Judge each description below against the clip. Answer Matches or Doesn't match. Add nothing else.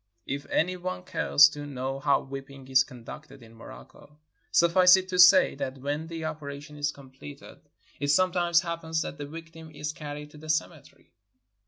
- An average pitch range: Matches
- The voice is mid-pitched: Matches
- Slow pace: Doesn't match